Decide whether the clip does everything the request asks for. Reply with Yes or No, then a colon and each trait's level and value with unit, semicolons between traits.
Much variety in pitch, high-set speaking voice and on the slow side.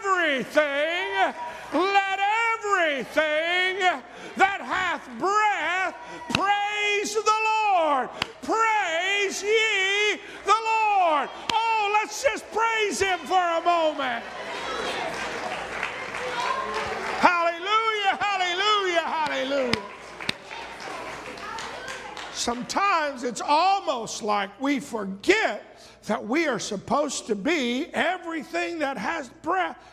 Yes: wide, 5.8 semitones; very high, 350 Hz; slow, 80 wpm